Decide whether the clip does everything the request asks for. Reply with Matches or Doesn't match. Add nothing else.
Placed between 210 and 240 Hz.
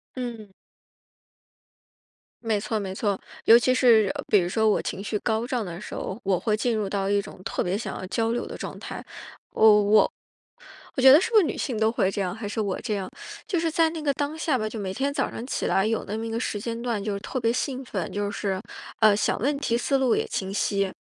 Matches